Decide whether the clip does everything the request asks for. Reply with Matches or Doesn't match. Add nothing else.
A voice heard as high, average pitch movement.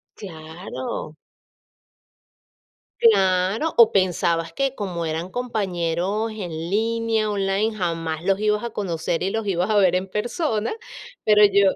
Matches